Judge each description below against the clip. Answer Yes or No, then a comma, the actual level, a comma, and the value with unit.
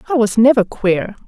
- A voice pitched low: No, high, 225 Hz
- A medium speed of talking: Yes, average, 190 wpm